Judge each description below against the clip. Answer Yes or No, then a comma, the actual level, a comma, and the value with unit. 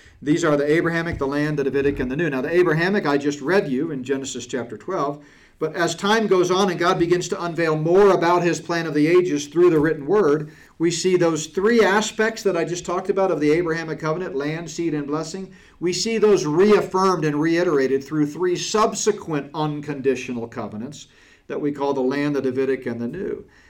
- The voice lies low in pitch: No, medium, 165 Hz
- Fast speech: Yes, fast, 210 wpm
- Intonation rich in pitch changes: No, average, 4.0 semitones